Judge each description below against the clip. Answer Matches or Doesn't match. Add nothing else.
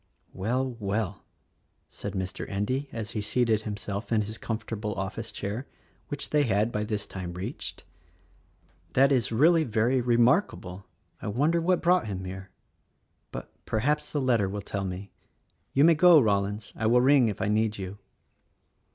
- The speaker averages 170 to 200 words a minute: Doesn't match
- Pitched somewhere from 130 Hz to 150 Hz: Doesn't match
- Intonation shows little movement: Doesn't match